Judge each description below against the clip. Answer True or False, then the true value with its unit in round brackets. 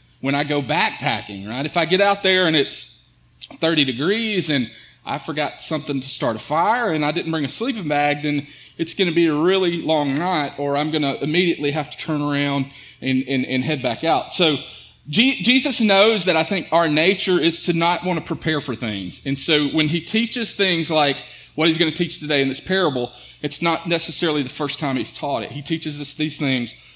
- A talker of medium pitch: True (155 Hz)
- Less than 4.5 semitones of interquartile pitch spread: True (3.5 semitones)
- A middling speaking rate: False (225 wpm)